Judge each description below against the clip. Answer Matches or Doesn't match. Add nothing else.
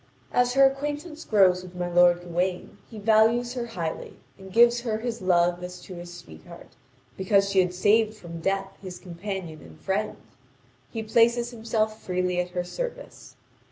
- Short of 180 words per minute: Matches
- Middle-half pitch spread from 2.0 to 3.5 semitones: Doesn't match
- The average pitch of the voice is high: Matches